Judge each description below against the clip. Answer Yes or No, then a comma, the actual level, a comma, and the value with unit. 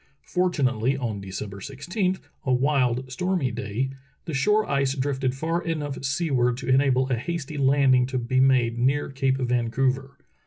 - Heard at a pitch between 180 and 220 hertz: No, low, 135 Hz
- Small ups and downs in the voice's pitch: Yes, narrow, 2.3 semitones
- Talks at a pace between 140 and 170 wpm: Yes, average, 155 wpm